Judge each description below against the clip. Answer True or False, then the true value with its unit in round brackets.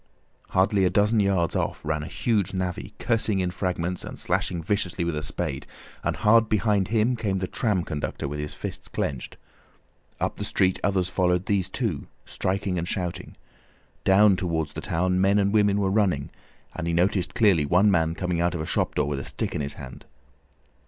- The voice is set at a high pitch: False (95 Hz)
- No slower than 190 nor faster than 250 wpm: True (195 wpm)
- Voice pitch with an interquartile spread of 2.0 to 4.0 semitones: True (3.1 semitones)